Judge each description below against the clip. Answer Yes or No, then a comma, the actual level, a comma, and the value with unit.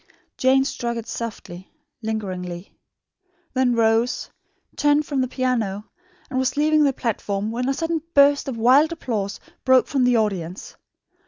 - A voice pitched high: Yes, high, 245 Hz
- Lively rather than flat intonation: No, average, 4.1 semitones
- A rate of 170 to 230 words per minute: No, average, 145 wpm